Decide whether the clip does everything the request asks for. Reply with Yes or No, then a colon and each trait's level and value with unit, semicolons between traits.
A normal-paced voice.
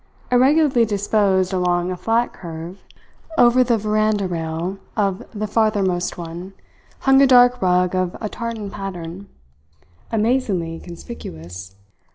No: slow, 120 wpm